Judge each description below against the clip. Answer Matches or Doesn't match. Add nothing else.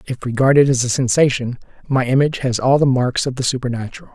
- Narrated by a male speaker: Matches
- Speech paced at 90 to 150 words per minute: Doesn't match